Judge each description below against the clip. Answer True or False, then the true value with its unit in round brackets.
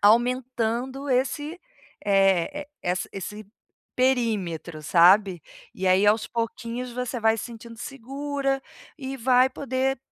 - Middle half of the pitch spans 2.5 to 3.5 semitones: False (4.3 semitones)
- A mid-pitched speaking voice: False (235 Hz)